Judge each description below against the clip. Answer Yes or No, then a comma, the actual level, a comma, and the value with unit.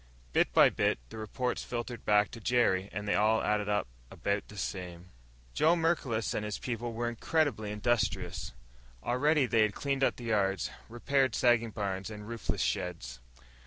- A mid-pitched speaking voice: No, low, 110 Hz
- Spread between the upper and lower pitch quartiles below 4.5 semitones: Yes, average, 3.1 semitones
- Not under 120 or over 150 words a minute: No, average, 165 wpm